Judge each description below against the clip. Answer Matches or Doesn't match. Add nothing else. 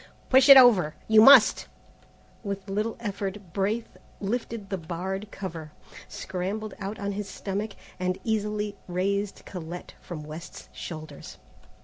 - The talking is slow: Matches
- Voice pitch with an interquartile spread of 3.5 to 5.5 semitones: Doesn't match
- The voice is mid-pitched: Doesn't match